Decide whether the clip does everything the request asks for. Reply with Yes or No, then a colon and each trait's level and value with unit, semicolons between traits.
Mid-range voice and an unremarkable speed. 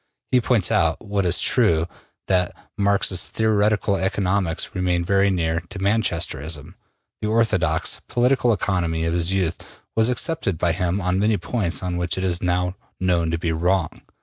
No: very low, 90 Hz; average, 160 wpm